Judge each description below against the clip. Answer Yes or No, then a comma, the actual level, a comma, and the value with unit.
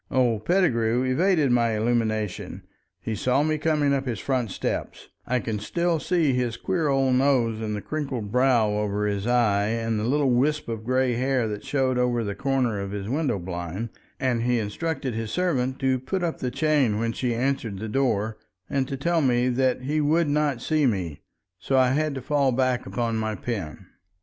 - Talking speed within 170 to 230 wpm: Yes, average, 190 wpm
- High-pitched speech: No, low, 125 Hz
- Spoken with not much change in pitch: No, average, 3.8 semitones